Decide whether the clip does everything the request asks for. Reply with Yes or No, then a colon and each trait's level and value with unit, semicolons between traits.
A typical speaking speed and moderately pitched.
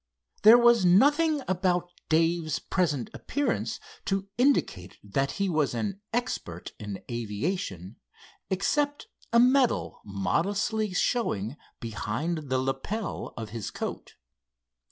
No: slow, 110 wpm; medium, 175 Hz